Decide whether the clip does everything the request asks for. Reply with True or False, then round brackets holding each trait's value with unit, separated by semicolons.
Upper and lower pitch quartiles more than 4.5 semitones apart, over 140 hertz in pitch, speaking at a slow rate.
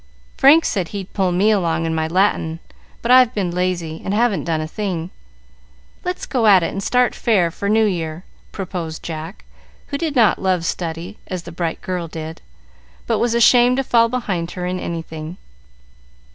False (5.0 semitones; 185 Hz; 180 wpm)